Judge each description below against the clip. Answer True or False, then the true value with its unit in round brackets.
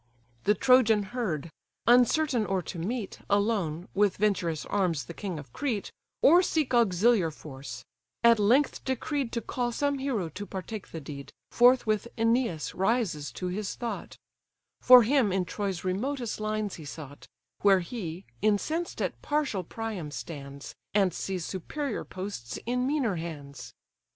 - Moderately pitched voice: False (205 Hz)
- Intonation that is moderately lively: False (6.1 semitones)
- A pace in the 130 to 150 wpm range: True (145 wpm)